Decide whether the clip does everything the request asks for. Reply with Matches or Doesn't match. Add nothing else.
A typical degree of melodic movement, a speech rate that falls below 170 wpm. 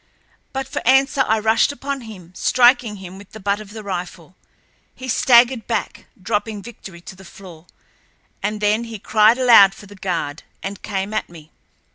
Doesn't match